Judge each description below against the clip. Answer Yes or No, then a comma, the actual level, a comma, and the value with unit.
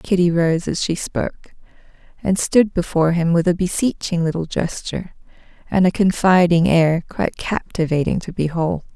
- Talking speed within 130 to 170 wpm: Yes, average, 145 wpm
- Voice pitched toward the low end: No, medium, 175 Hz